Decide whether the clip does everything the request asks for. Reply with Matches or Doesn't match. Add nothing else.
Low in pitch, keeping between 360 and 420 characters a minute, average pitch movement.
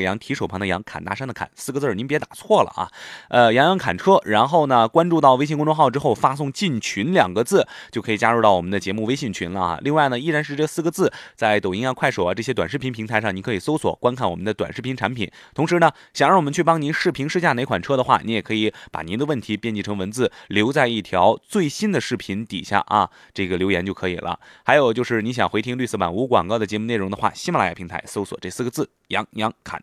Doesn't match